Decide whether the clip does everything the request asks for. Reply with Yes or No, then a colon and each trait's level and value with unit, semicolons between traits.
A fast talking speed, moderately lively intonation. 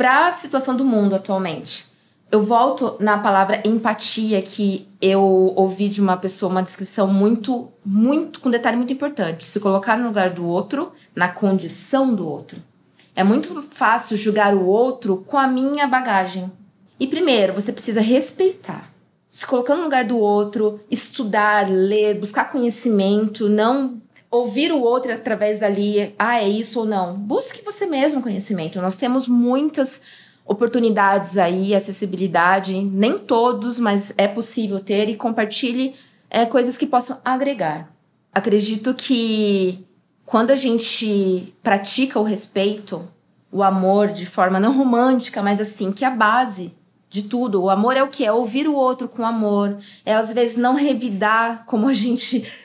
No: average, 155 wpm; average, 4.2 semitones